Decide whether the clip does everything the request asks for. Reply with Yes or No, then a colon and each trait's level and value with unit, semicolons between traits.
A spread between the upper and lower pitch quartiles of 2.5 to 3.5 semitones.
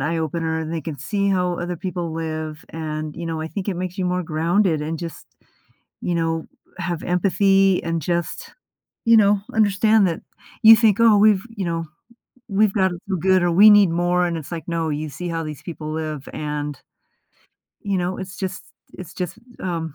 Yes: average, 3.1 semitones